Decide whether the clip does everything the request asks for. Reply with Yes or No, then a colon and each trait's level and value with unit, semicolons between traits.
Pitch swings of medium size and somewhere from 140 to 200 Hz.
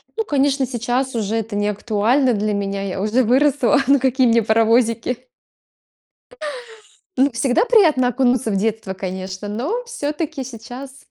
No: average, 4.1 semitones; high, 240 Hz